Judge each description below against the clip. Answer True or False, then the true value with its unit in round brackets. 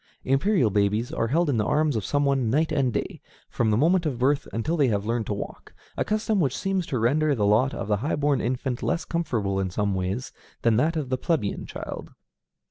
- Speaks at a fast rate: True (225 wpm)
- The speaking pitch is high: False (130 Hz)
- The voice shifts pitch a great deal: True (5.9 semitones)